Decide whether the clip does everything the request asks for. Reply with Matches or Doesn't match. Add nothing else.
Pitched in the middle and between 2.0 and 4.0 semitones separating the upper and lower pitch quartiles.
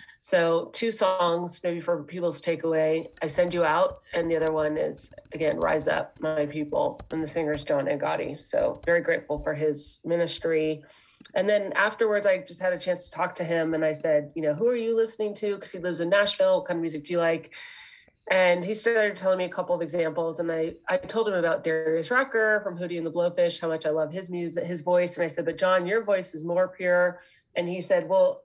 Matches